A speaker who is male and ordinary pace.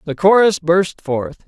Yes: male; average, 165 wpm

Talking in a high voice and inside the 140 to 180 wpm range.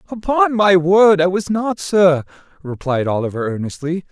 No: medium, 175 Hz; average, 145 wpm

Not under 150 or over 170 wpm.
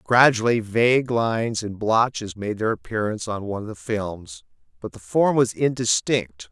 Yes: average, 165 wpm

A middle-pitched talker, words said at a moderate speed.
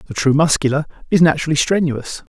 Yes: medium, 150 Hz; average, 155 wpm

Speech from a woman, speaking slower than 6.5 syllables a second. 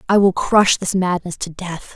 Yes: female; 4.5 syllables/s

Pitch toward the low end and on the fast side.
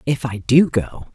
Yes: low, 130 Hz; fast, 210 wpm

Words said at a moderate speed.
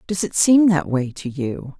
No: fast, 235 wpm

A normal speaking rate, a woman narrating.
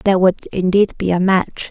No: fast, 210 wpm; female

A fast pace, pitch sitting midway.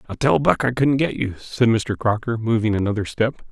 No: fast, 220 wpm; low, 115 Hz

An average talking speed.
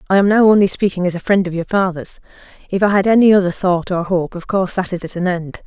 No: fast, 275 wpm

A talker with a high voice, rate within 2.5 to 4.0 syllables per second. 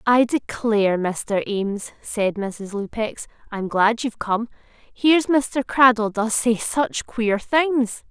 Yes: high, 225 Hz; 3.6 syllables/s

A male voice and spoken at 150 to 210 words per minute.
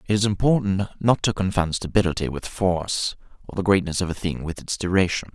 Yes: male; average, 200 wpm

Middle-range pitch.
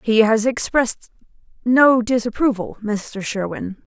No: high, 230 Hz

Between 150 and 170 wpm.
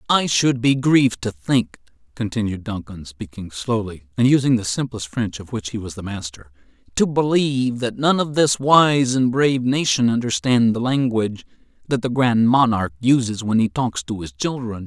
No: average, 180 wpm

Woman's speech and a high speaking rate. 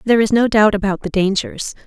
Yes: female; fast, 225 wpm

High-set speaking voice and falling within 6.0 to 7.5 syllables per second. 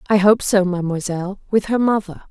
Yes: high, 195 Hz; 6.2 syllables/s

